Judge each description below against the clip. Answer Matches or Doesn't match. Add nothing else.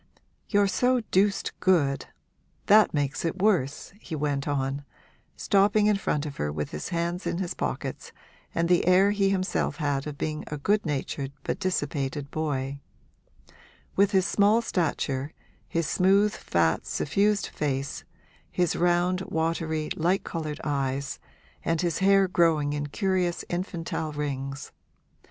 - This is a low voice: Doesn't match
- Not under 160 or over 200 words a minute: Doesn't match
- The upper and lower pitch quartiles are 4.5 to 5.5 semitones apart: Matches